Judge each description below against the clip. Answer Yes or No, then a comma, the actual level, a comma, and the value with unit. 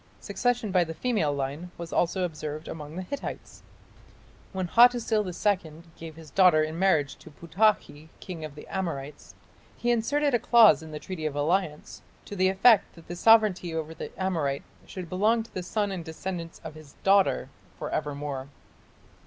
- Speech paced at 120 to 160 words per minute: No, average, 170 wpm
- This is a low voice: No, medium, 175 Hz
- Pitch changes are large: No, average, 4.5 semitones